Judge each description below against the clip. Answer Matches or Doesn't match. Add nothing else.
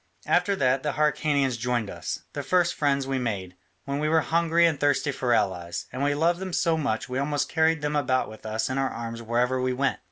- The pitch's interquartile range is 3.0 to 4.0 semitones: Matches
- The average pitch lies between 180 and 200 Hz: Doesn't match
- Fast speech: Matches